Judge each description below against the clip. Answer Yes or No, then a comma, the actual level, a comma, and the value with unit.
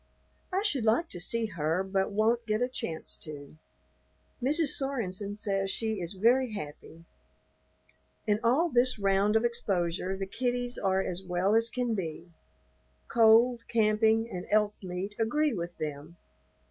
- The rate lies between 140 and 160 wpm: Yes, average, 145 wpm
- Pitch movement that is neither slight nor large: Yes, average, 4.2 semitones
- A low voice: No, high, 210 Hz